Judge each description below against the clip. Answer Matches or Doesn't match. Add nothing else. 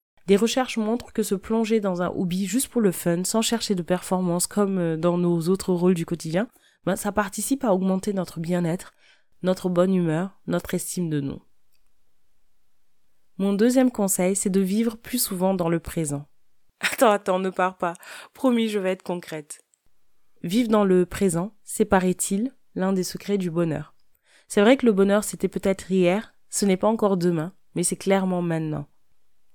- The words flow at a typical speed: Matches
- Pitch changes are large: Doesn't match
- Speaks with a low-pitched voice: Doesn't match